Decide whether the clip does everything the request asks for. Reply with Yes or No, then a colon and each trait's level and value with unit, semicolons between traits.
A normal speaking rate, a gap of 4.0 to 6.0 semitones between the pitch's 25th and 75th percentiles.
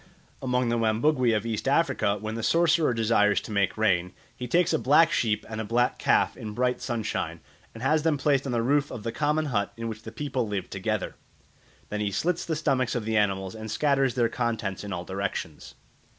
No: fast, 210 wpm; average, 4.6 semitones